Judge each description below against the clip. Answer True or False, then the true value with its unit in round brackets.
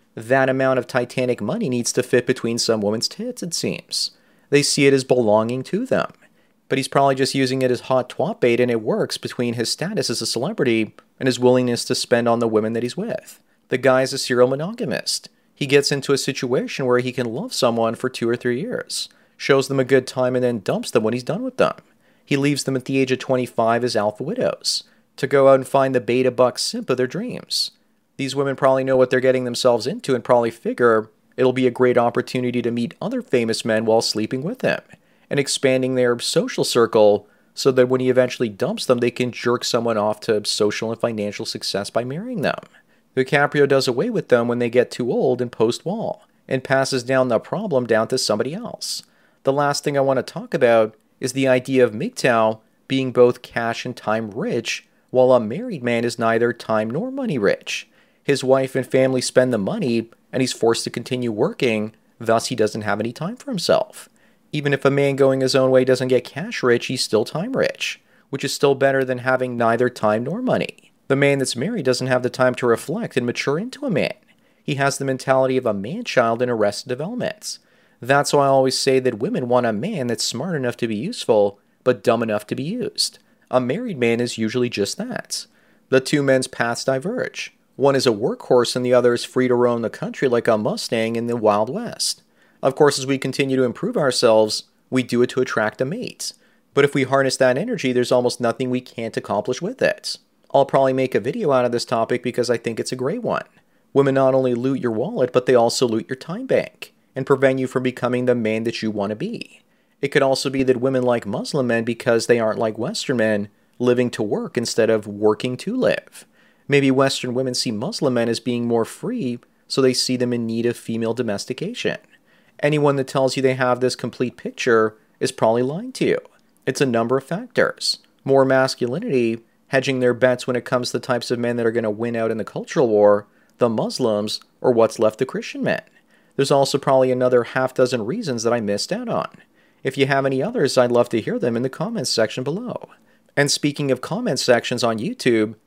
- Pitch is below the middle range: True (125 Hz)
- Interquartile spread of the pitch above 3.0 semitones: False (2.4 semitones)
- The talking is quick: True (220 wpm)